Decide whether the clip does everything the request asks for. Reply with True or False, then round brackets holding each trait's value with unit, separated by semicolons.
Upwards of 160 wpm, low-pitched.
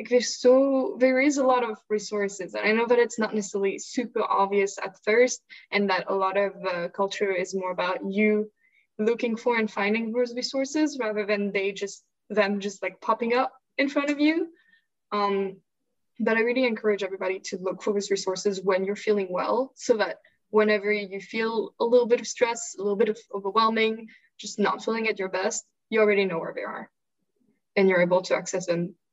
False (200 wpm; 215 Hz)